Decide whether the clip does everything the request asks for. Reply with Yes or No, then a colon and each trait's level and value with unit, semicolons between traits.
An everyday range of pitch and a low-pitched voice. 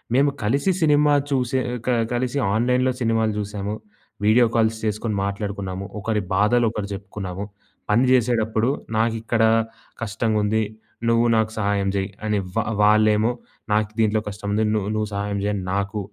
No: narrow, 2.2 semitones; low, 110 Hz